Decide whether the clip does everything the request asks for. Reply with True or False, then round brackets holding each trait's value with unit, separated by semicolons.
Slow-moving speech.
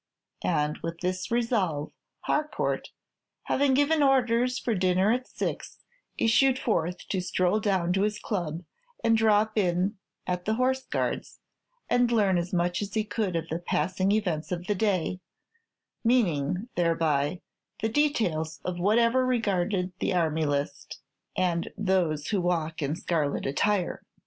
False (145 wpm)